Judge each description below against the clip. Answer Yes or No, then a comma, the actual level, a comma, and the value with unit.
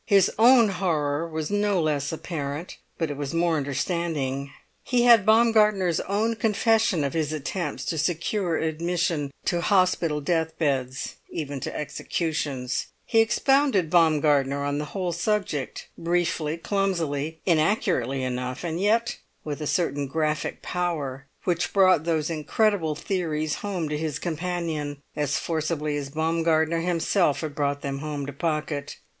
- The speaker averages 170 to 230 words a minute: No, average, 140 wpm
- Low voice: No, medium, 160 Hz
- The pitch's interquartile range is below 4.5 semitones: Yes, average, 3.8 semitones